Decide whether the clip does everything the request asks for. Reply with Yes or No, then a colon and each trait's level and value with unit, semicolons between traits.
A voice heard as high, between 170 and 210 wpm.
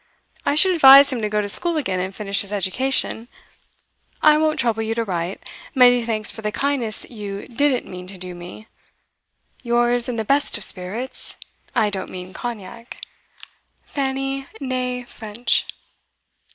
No: high, 230 Hz; average, 155 wpm